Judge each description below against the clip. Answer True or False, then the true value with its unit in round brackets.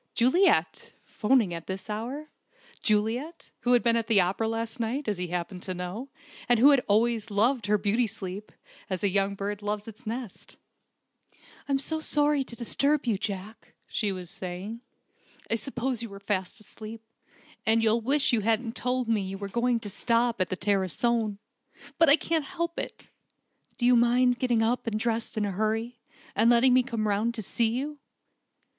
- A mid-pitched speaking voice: False (225 Hz)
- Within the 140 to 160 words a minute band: False (180 wpm)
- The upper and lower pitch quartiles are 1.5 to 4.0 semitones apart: True (3.3 semitones)